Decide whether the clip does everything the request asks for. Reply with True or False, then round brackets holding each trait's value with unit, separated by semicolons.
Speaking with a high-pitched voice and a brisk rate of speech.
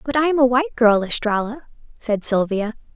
False (235 Hz; 185 wpm)